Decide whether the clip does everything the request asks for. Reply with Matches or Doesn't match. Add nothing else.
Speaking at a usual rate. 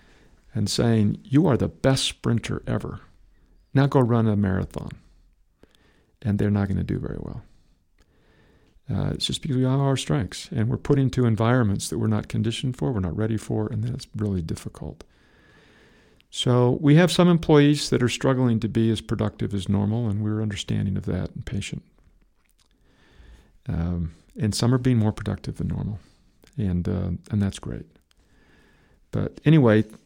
Matches